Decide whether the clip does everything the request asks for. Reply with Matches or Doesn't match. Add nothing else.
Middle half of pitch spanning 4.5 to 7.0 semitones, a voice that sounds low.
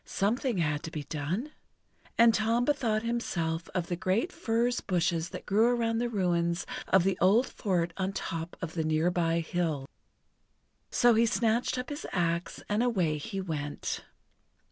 Doesn't match